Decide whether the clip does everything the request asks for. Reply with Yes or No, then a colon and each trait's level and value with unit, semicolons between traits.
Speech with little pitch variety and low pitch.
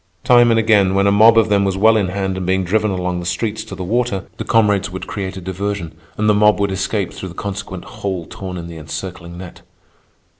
Yes: narrow, 2.3 semitones; very low, 95 Hz